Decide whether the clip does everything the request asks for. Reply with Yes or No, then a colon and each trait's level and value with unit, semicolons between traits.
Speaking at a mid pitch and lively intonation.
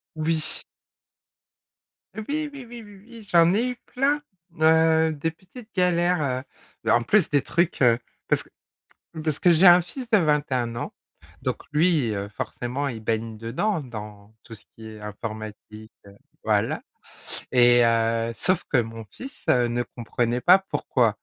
Yes: medium, 145 Hz; wide, 7.7 semitones